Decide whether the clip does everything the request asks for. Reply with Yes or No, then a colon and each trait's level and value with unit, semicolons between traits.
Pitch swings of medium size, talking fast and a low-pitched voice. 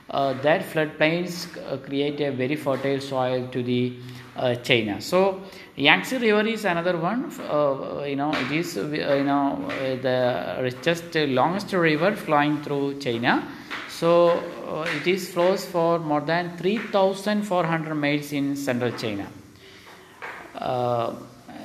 No: average, 4.8 semitones; fast, 140 wpm; medium, 150 Hz